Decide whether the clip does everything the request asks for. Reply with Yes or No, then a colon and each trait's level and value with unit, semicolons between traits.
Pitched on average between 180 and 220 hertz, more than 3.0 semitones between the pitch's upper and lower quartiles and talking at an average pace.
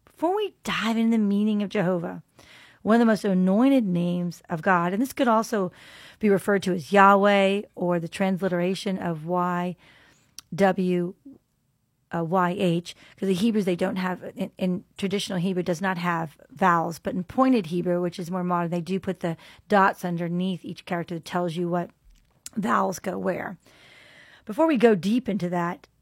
No: medium, 185 Hz; narrow, 2.5 semitones; average, 170 wpm